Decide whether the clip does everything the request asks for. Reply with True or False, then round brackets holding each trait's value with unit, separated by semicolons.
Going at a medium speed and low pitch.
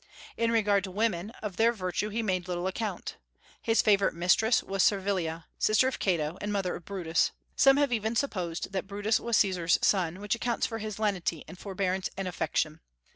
False (185 wpm; 195 Hz)